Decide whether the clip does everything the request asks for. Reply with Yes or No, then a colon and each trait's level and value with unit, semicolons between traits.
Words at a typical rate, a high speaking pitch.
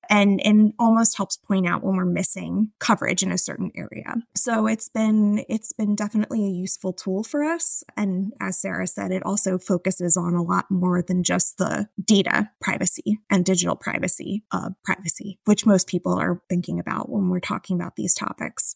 Yes: average, 185 wpm; high, 195 Hz